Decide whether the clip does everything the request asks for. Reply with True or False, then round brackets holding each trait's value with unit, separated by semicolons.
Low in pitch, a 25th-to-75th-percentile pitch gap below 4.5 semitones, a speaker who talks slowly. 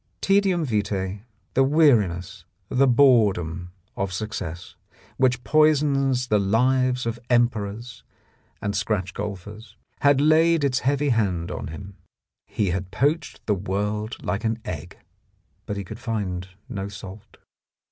False (110 Hz; 5.1 semitones; 130 wpm)